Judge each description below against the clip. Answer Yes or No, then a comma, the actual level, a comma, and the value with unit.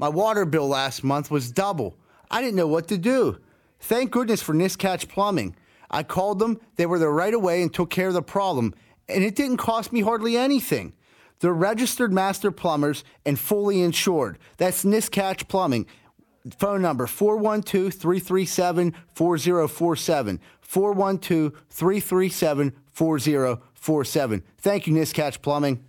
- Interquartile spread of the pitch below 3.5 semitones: No, average, 4.8 semitones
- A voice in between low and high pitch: Yes, medium, 180 Hz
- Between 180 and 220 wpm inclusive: No, average, 140 wpm